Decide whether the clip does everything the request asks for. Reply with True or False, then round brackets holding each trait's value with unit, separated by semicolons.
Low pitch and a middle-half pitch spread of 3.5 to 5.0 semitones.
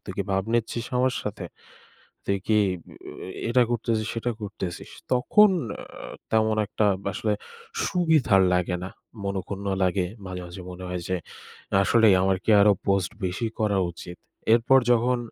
True (105 Hz; 4.0 semitones)